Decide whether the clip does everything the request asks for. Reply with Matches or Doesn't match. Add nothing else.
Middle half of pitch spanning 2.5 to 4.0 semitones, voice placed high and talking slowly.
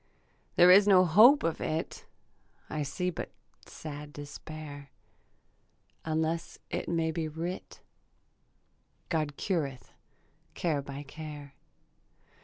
Doesn't match